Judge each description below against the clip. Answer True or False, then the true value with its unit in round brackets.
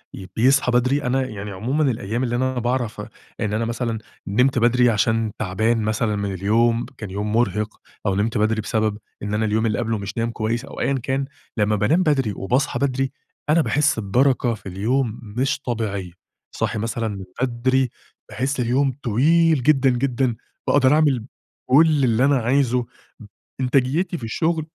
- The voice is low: True (120 Hz)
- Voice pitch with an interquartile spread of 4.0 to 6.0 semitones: False (3.6 semitones)